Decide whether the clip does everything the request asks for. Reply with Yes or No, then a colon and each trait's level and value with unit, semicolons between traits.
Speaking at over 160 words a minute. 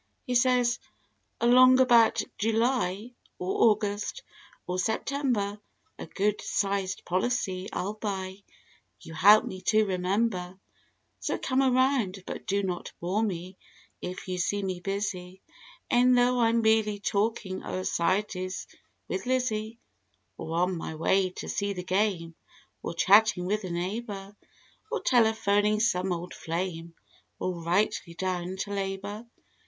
No: slow, 135 wpm